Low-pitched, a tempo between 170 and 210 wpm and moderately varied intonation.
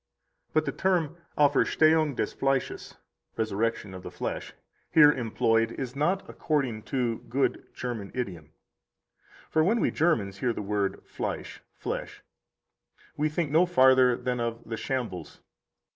No: low, 130 Hz; average, 140 wpm; average, 5.0 semitones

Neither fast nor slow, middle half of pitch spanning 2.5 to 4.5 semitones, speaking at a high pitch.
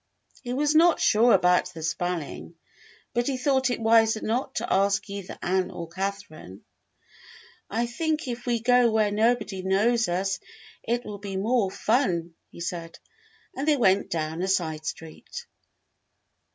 No: average, 150 wpm; average, 5.1 semitones; high, 205 Hz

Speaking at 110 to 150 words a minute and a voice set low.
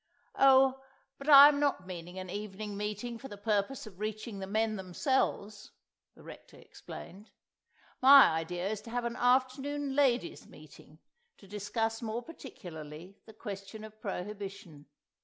No: average, 145 wpm; high, 215 Hz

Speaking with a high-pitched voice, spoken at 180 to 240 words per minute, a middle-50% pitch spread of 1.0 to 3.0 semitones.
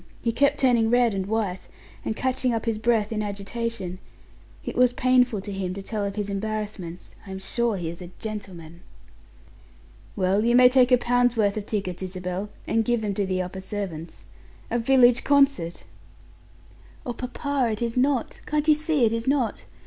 No: high, 220 Hz; average, 185 wpm; average, 4.1 semitones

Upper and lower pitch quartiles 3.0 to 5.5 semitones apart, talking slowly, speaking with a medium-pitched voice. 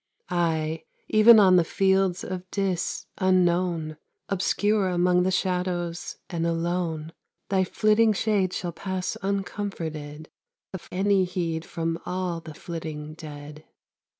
No: narrow, 2.6 semitones; slow, 120 wpm; medium, 180 Hz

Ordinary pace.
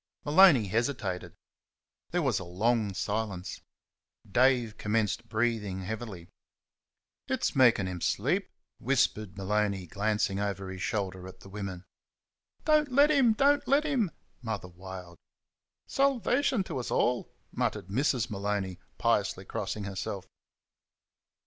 No: slow, 115 wpm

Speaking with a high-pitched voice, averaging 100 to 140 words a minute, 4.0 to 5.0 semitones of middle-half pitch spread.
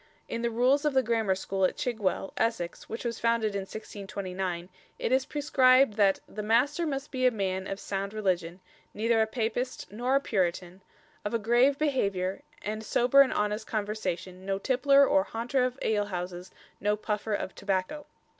No: high, 220 Hz; average, 175 wpm; average, 4.6 semitones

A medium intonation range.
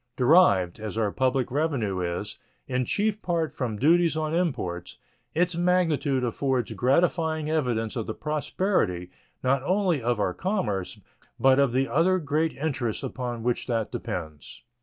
No: wide, 6.3 semitones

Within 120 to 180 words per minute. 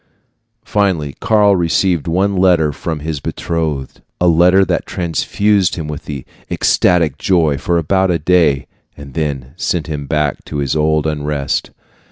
Yes: average, 145 wpm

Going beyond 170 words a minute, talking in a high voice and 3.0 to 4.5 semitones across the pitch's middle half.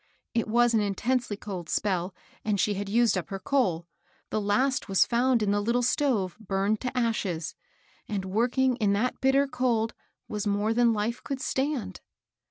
Yes: average, 180 wpm; high, 220 Hz; average, 3.6 semitones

